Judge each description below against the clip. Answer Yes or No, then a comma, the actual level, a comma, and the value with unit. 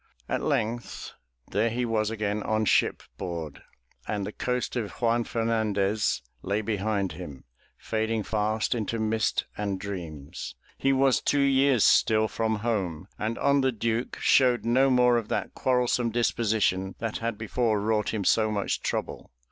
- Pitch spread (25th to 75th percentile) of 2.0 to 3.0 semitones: Yes, narrow, 2.5 semitones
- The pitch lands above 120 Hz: No, low, 110 Hz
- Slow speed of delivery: No, average, 150 wpm